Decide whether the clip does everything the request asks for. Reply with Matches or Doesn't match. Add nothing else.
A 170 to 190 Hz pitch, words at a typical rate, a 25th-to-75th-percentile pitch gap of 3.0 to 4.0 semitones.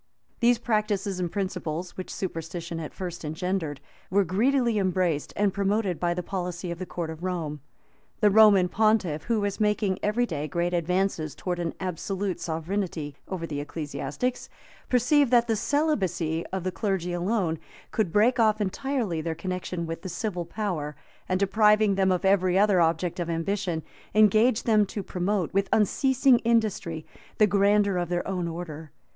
Matches